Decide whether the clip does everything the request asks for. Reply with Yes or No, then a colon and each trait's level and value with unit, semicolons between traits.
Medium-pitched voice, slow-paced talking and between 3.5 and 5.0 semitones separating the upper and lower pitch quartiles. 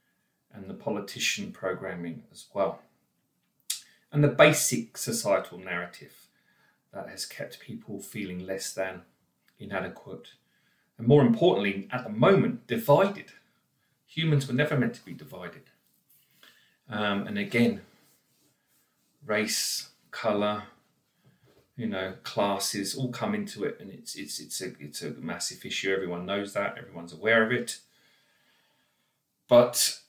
No: low, 100 Hz; slow, 125 wpm; average, 4.6 semitones